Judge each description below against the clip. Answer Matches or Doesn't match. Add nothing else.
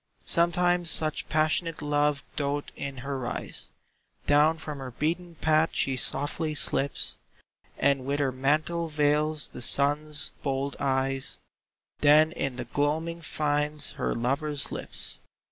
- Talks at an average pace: Doesn't match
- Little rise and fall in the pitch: Matches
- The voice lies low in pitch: Doesn't match